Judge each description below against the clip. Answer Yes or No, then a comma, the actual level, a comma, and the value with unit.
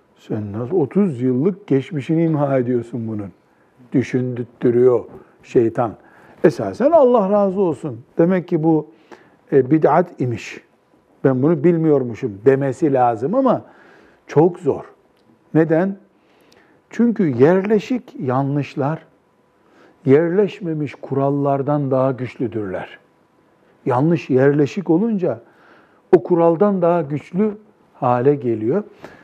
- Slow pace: Yes, slow, 90 wpm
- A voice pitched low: No, medium, 150 Hz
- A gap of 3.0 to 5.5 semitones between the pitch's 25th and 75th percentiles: Yes, average, 5.2 semitones